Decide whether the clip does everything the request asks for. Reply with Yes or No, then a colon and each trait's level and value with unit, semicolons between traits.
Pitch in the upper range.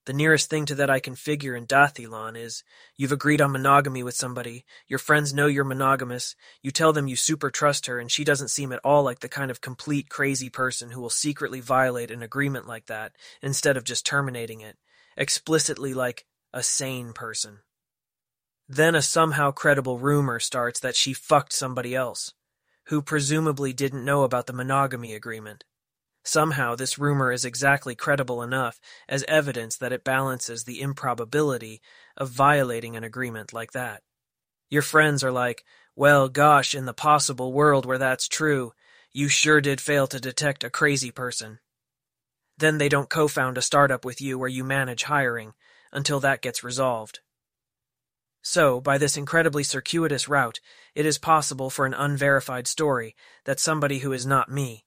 No: low, 135 Hz